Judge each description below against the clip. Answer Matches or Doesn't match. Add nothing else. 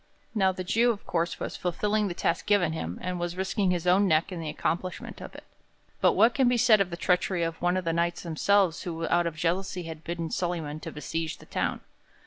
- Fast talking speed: Matches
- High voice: Doesn't match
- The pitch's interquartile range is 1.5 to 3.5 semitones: Matches